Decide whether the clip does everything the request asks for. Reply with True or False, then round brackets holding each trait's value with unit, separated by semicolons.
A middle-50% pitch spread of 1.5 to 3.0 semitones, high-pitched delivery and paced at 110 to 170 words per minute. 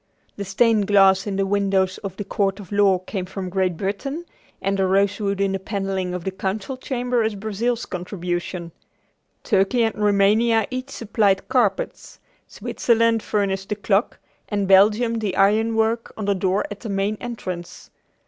True (2.5 semitones; 200 Hz; 165 wpm)